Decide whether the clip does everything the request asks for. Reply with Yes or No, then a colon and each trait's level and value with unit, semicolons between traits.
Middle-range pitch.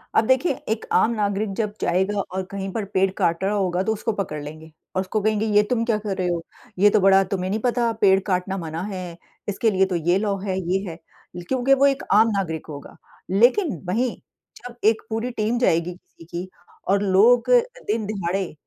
No: high, 195 Hz